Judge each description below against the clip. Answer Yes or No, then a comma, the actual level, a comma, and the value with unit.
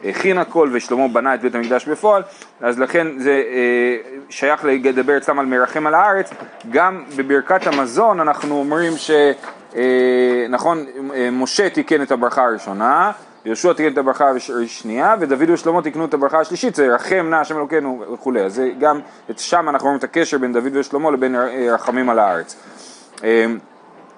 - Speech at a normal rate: No, fast, 160 wpm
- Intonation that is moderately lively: Yes, average, 3.6 semitones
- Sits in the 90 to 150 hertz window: Yes, medium, 140 Hz